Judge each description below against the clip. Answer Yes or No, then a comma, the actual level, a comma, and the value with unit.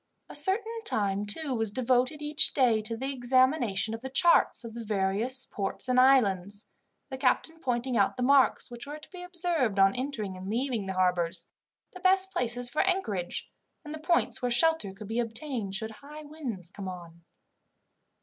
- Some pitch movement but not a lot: No, wide, 6.3 semitones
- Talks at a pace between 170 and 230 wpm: Yes, average, 180 wpm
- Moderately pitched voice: No, high, 245 Hz